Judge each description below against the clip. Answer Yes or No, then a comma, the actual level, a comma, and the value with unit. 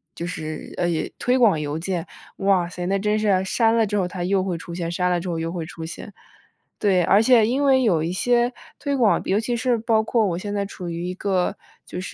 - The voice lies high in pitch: Yes, high, 195 Hz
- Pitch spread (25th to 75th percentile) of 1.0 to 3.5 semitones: No, average, 4.2 semitones